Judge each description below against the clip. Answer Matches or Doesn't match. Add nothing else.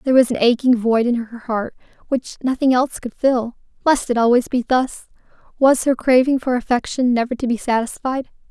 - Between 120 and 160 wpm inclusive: Doesn't match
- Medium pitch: Doesn't match